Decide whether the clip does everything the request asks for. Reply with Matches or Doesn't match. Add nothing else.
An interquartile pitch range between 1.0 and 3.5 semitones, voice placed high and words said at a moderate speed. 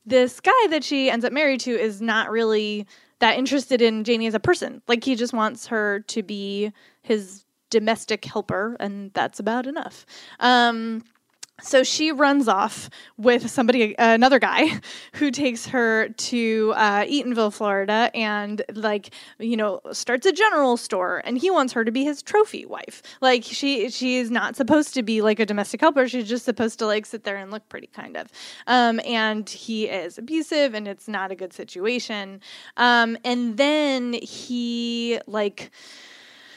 Matches